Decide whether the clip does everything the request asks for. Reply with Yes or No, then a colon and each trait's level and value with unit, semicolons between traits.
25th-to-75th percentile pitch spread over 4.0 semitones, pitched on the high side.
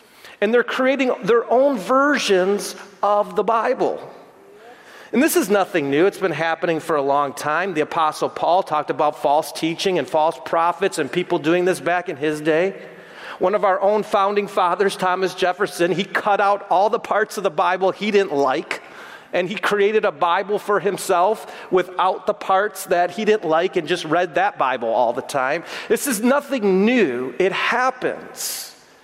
No: average, 3.4 semitones; high, 195 Hz